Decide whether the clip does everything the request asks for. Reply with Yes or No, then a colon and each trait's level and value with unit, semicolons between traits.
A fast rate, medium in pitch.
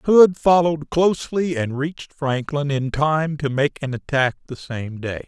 No: average, 170 wpm; medium, 145 Hz